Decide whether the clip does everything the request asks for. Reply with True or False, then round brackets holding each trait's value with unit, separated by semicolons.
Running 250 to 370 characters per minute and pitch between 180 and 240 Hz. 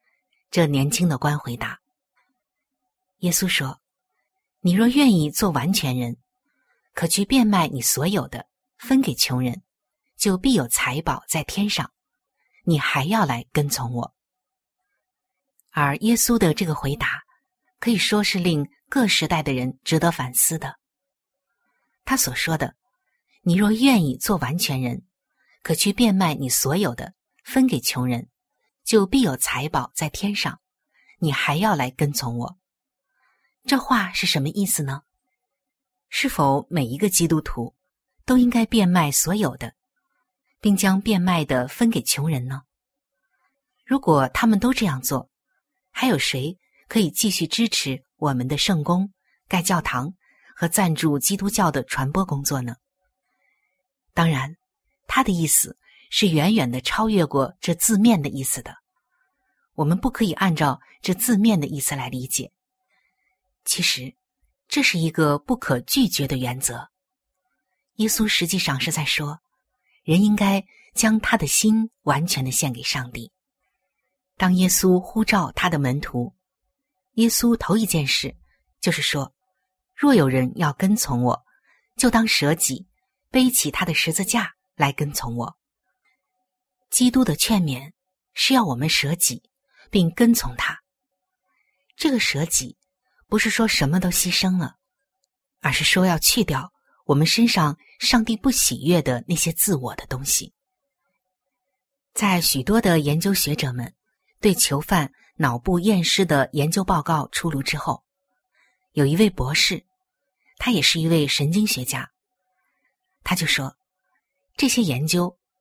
False (200 characters per minute; 185 Hz)